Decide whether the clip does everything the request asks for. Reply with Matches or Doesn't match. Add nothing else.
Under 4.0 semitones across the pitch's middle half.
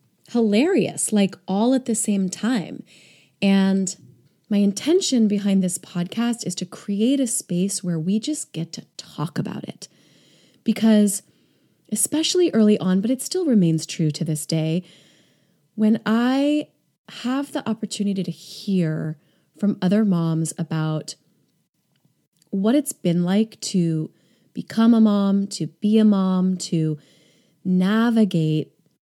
Doesn't match